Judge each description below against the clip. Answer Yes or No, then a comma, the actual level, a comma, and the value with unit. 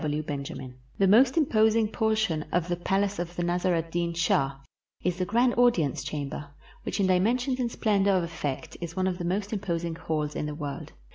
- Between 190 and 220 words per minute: Yes, fast, 205 wpm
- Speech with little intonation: No, average, 4.8 semitones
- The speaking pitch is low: No, medium, 175 Hz